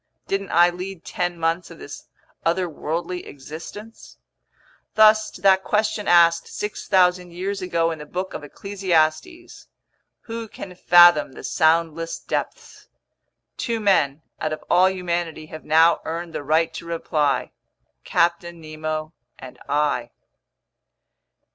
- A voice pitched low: No, medium, 170 Hz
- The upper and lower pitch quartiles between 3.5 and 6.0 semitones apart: No, average, 3.1 semitones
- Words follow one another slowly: Yes, slow, 120 wpm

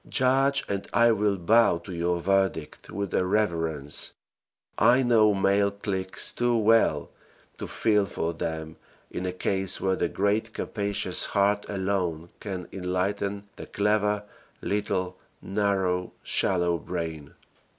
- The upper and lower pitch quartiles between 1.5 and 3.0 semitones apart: Yes, average, 2.7 semitones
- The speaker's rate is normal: No, slow, 130 wpm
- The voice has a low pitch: Yes, low, 100 Hz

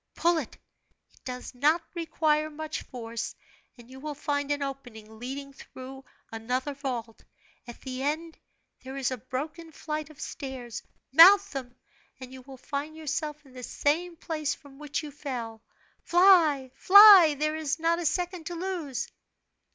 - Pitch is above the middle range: Yes, very high, 285 Hz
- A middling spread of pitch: Yes, average, 3.5 semitones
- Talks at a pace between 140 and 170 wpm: Yes, average, 160 wpm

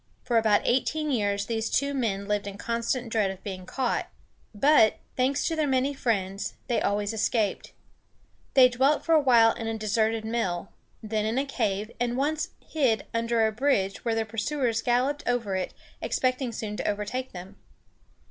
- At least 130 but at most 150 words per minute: No, average, 175 wpm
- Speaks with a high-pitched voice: Yes, high, 230 Hz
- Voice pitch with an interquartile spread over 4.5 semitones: No, average, 3.8 semitones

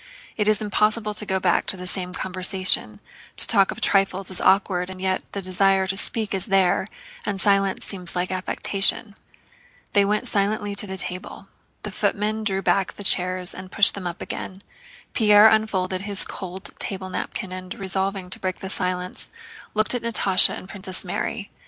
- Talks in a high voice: Yes, high, 195 Hz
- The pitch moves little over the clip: Yes, narrow, 1.7 semitones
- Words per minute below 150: No, average, 175 wpm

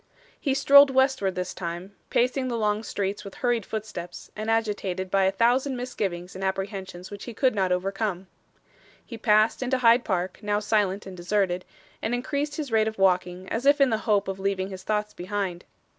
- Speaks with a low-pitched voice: No, high, 205 Hz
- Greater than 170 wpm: Yes, average, 190 wpm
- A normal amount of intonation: Yes, average, 3.8 semitones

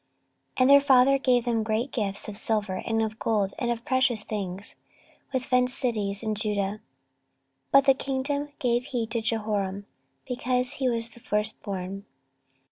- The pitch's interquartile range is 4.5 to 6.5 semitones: No, average, 3.3 semitones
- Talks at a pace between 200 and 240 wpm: No, average, 160 wpm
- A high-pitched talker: Yes, high, 230 Hz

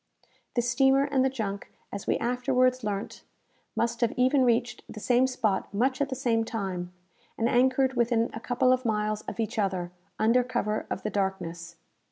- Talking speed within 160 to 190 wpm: Yes, average, 180 wpm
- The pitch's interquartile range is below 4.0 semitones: Yes, average, 3.4 semitones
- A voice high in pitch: Yes, high, 235 Hz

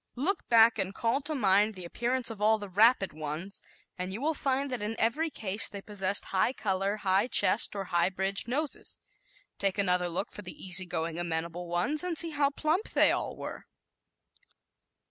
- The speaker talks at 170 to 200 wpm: Yes, average, 185 wpm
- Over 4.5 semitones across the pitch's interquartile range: Yes, average, 5.2 semitones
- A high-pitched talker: Yes, high, 205 Hz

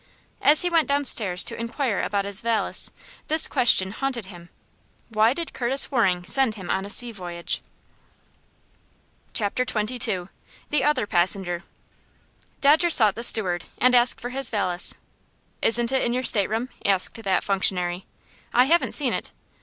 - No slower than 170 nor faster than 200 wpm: No, average, 150 wpm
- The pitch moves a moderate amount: Yes, average, 5.0 semitones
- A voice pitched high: Yes, high, 225 Hz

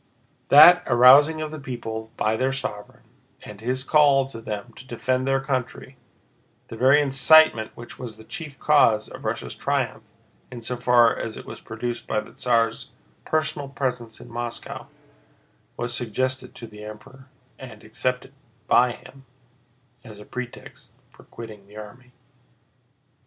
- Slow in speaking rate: No, average, 145 wpm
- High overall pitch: No, low, 125 Hz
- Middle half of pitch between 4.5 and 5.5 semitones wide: No, average, 3.0 semitones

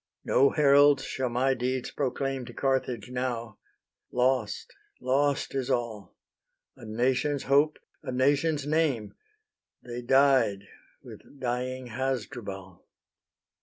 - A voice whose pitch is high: No, low, 130 Hz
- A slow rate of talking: Yes, slow, 105 wpm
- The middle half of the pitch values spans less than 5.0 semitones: Yes, narrow, 2.4 semitones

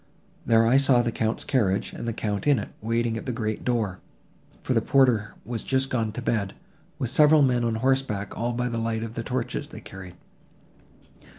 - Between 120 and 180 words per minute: No, average, 190 wpm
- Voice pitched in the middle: No, low, 115 Hz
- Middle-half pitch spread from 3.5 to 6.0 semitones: No, average, 2.7 semitones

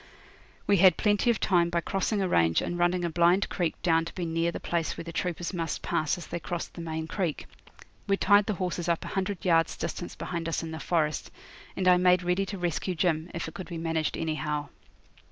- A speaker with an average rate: No, fast, 225 wpm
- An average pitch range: No, narrow, 1.9 semitones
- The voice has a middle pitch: Yes, medium, 175 Hz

